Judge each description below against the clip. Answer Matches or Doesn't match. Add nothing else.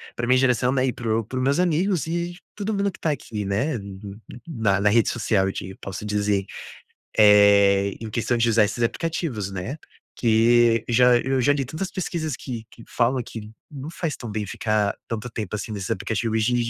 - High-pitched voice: Doesn't match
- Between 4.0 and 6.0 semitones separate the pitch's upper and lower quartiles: Matches